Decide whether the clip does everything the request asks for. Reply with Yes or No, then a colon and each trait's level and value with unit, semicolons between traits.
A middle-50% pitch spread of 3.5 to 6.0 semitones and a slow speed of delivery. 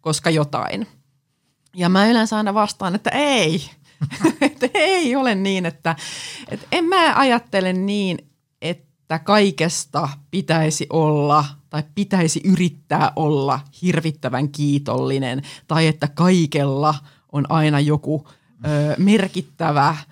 No: average, 4.6 semitones; average, 110 wpm